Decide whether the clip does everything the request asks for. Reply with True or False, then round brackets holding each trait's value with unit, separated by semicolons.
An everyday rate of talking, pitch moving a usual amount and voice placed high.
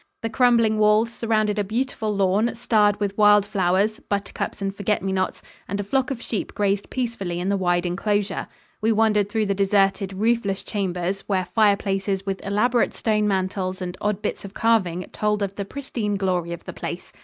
False (185 wpm; 2.0 semitones; 205 Hz)